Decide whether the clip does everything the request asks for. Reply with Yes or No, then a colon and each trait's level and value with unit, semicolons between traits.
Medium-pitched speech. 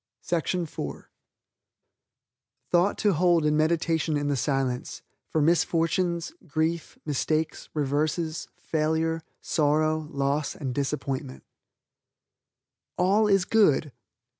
Yes: medium, 155 Hz